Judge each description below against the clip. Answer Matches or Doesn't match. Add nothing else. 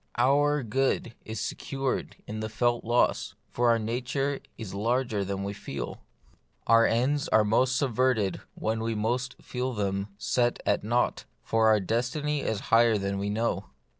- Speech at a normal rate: Matches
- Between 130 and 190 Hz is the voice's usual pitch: Doesn't match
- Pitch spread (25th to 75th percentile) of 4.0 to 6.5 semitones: Doesn't match